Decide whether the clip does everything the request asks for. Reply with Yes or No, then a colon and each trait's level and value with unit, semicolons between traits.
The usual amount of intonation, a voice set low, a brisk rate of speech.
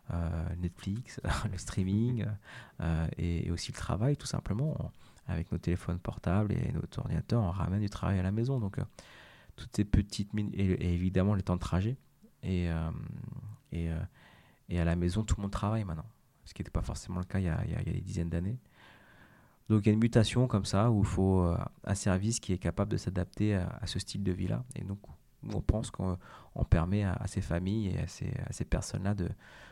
Yes: average, 4.2 semitones; low, 100 Hz; fast, 225 wpm